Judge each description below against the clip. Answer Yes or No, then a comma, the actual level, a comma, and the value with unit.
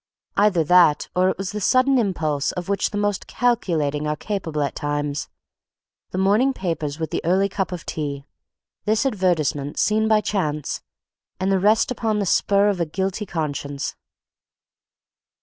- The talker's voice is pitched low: No, medium, 185 Hz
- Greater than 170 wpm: No, average, 160 wpm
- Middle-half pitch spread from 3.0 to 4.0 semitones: No, average, 5.3 semitones